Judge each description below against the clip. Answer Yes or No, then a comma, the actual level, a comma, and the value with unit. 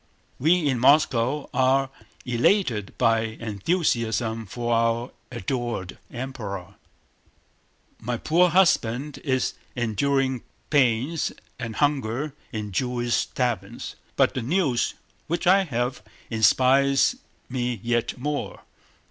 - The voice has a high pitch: No, low, 125 Hz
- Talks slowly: Yes, slow, 100 wpm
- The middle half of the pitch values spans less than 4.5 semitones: Yes, average, 3.4 semitones